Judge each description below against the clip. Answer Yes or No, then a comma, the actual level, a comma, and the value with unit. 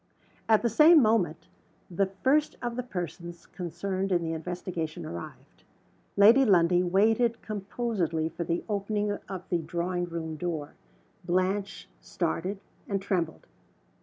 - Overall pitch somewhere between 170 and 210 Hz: Yes, medium, 185 Hz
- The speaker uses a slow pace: Yes, slow, 130 wpm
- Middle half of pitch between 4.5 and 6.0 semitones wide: No, average, 3.4 semitones